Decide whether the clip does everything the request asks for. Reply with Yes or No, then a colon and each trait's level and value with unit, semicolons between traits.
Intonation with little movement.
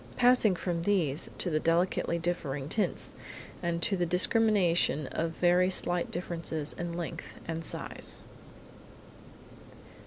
Yes: narrow, 1.8 semitones